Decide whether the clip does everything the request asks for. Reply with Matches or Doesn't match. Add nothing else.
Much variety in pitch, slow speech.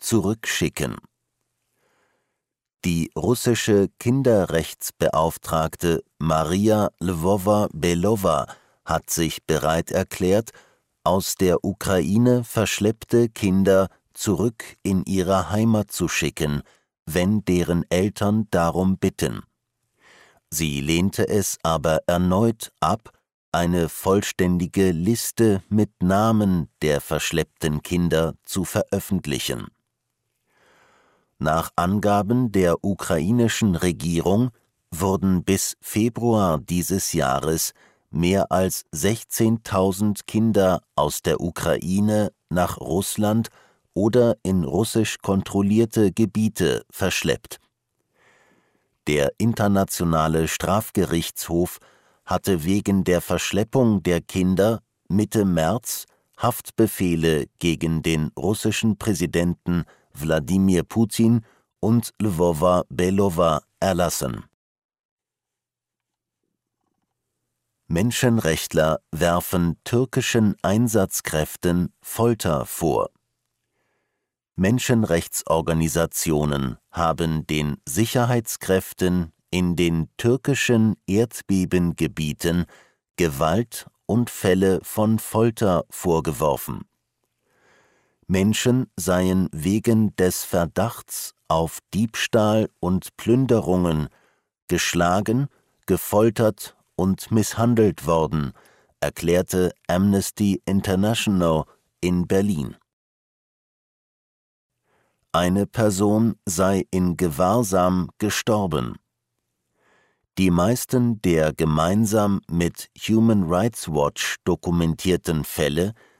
Doesn't match